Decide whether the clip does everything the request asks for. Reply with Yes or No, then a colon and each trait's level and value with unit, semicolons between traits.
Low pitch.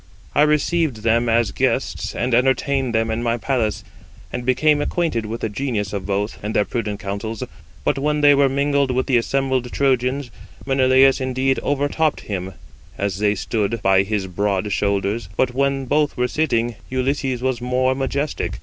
Yes: low, 125 Hz